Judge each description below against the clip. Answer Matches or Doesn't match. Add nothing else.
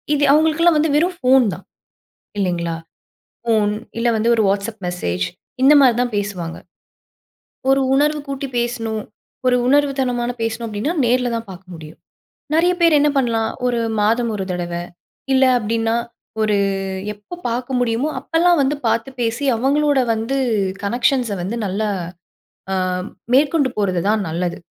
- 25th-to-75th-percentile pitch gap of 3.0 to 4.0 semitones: Doesn't match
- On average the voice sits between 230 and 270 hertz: Matches